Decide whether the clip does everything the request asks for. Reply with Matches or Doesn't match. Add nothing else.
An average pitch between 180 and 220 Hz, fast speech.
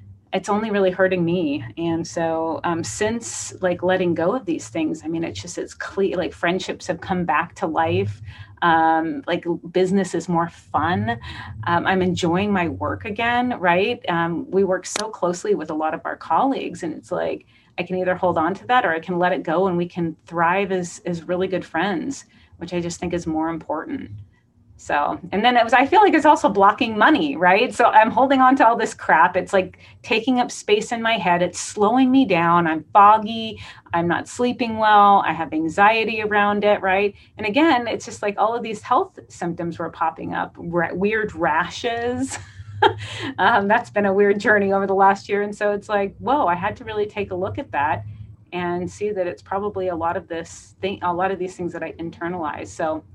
Matches